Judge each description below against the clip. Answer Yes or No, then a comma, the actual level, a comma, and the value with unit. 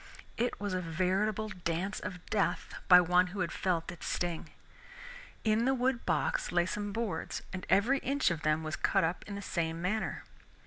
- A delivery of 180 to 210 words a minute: Yes, average, 185 wpm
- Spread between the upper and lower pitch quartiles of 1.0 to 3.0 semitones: No, average, 3.8 semitones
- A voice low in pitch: No, medium, 185 Hz